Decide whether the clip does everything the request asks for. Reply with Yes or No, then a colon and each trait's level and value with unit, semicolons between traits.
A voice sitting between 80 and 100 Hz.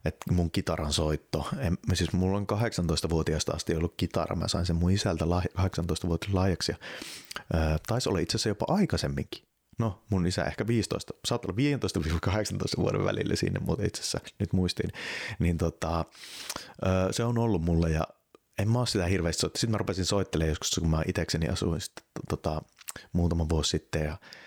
Yes: very low, 90 Hz